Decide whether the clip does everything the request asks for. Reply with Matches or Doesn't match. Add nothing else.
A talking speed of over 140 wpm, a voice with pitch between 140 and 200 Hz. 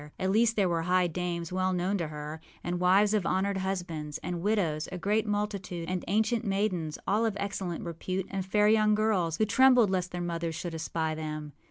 Matches